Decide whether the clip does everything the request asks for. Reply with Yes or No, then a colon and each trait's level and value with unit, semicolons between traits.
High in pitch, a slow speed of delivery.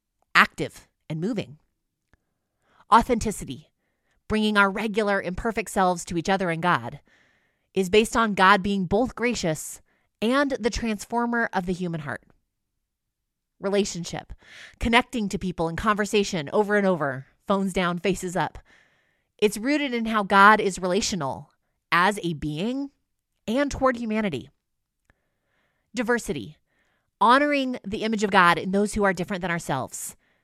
Yes: high, 200 Hz; slow, 130 wpm